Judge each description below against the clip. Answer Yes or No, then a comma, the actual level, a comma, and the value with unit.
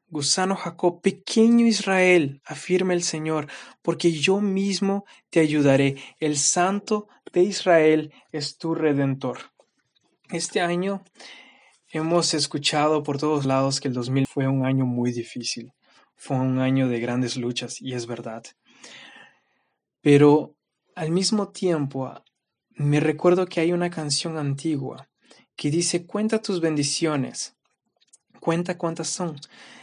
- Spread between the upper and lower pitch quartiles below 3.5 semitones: No, average, 4.8 semitones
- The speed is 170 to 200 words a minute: No, slow, 125 wpm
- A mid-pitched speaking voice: Yes, medium, 155 Hz